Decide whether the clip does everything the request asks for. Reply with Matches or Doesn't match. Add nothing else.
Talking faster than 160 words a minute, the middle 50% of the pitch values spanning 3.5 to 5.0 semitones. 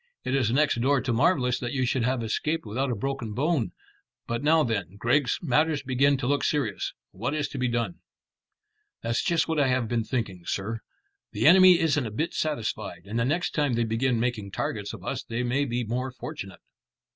Matches